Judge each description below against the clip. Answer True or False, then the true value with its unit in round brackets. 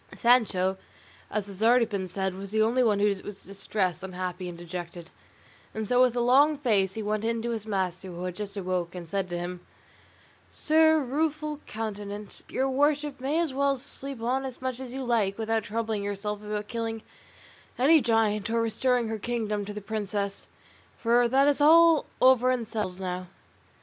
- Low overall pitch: False (220 Hz)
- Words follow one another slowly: False (185 wpm)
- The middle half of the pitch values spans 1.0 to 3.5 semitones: False (4.3 semitones)